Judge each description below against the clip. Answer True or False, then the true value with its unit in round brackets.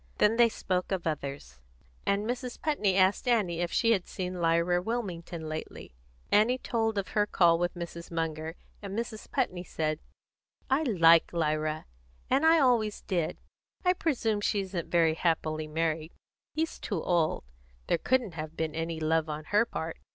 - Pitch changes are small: False (5.2 semitones)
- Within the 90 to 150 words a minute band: False (165 wpm)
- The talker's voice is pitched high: False (175 Hz)